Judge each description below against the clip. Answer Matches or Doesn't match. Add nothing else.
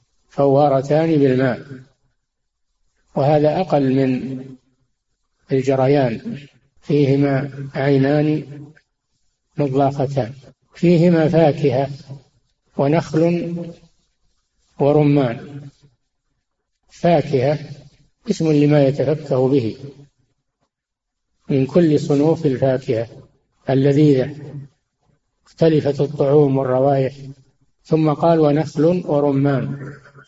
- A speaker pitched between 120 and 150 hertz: Matches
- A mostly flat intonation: Matches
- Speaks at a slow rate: Matches